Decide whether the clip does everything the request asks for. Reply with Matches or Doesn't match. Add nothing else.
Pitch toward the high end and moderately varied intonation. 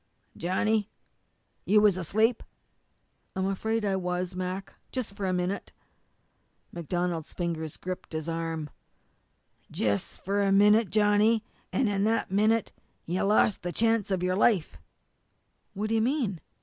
Matches